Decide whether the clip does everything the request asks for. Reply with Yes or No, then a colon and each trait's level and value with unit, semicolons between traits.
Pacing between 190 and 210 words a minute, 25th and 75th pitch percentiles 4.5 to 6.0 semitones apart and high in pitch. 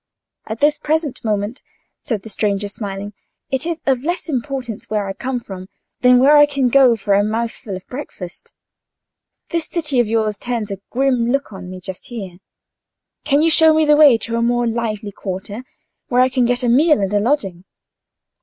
Yes: average, 195 wpm; average, 5.0 semitones; high, 235 Hz